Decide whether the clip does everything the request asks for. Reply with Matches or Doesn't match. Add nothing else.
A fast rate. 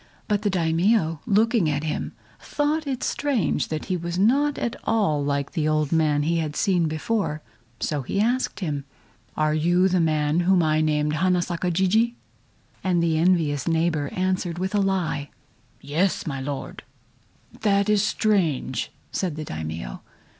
Doesn't match